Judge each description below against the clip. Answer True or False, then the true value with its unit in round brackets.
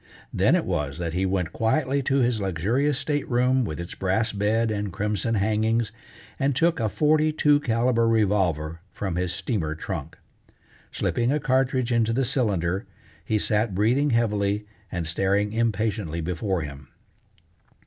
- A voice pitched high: False (110 Hz)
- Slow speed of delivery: False (150 wpm)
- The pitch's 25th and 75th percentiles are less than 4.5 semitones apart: False (4.8 semitones)